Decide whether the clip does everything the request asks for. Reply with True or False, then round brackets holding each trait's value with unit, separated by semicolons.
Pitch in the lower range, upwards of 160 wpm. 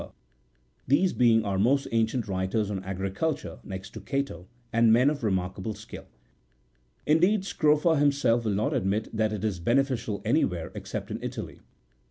True (110 Hz; 170 wpm)